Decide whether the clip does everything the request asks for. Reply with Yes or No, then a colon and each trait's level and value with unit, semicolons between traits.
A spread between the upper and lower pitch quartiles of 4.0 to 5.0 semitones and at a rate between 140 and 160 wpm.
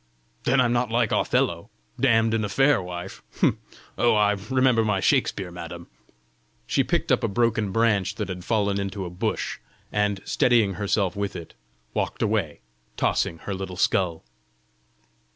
No: average, 3.3 semitones; average, 150 wpm